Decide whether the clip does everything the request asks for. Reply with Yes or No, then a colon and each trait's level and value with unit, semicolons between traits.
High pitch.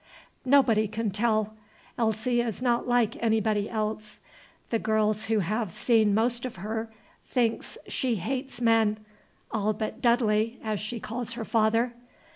Yes: high, 220 Hz